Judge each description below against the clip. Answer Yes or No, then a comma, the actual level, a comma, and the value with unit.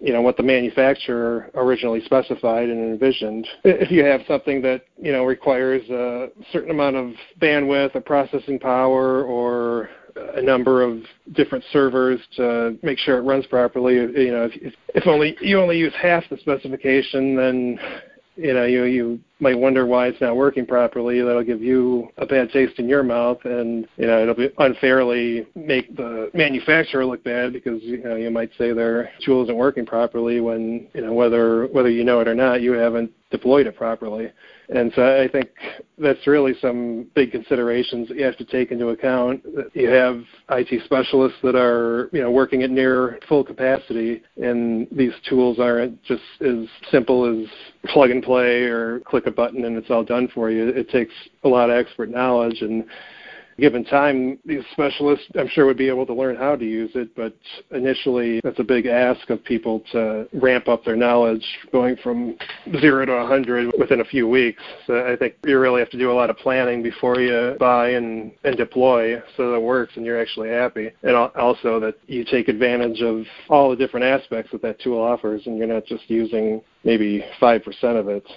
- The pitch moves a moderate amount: No, narrow, 2.0 semitones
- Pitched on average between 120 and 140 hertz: Yes, low, 125 Hz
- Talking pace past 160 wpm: Yes, average, 190 wpm